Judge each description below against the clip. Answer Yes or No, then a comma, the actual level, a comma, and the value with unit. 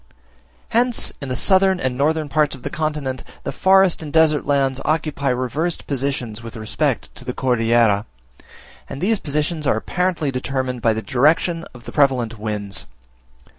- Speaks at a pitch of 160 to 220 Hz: No, medium, 140 Hz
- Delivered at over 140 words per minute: Yes, average, 160 wpm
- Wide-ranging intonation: No, average, 4.5 semitones